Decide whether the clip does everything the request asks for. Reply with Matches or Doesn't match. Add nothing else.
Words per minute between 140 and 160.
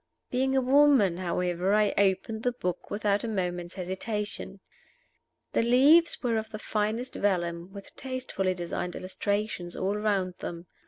Matches